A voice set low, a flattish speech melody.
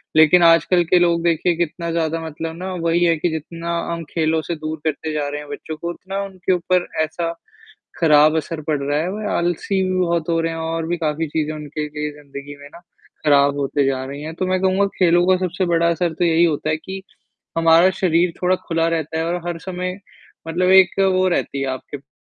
No: medium, 165 Hz; narrow, 2.3 semitones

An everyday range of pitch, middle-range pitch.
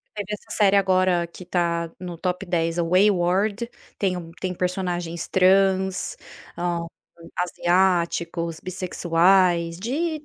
No: narrow, 1.9 semitones; medium, 180 Hz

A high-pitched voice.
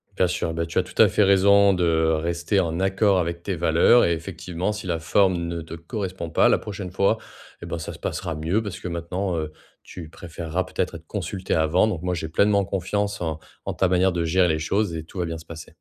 No: very low, 90 Hz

